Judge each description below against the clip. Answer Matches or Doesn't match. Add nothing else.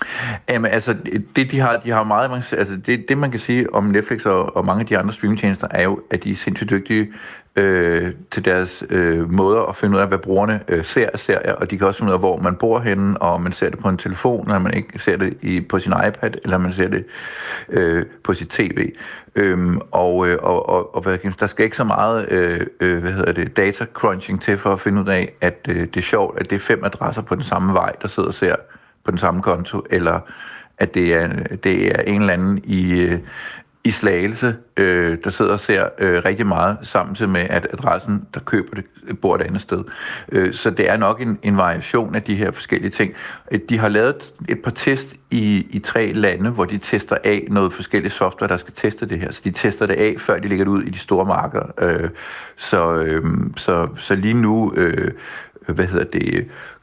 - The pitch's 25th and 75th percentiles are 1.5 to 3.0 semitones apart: Matches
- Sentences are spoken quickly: Matches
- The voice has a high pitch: Doesn't match